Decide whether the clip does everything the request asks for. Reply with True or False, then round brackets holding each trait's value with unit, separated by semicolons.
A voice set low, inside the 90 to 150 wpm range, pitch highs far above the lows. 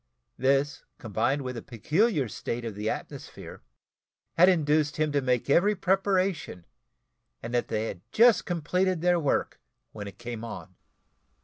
False (145 Hz; 145 wpm; 7.2 semitones)